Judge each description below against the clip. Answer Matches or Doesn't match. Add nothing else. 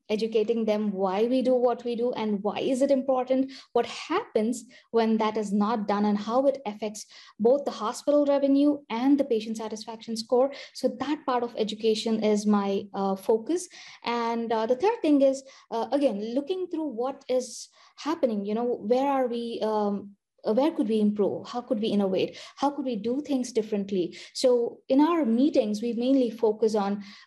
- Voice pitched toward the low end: Doesn't match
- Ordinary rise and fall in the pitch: Matches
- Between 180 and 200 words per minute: Matches